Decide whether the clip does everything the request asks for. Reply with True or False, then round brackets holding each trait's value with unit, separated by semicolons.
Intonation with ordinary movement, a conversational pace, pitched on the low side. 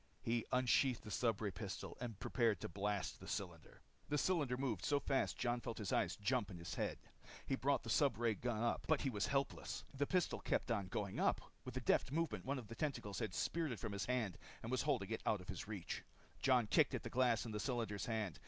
False (4.0 semitones; 230 wpm; 115 Hz)